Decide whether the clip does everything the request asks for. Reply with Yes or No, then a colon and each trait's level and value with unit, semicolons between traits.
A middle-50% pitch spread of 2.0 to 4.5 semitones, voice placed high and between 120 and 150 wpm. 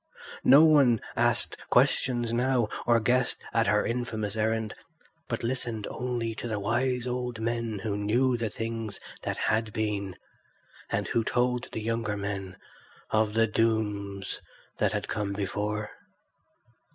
No: narrow, 2.4 semitones; low, 115 Hz; average, 140 wpm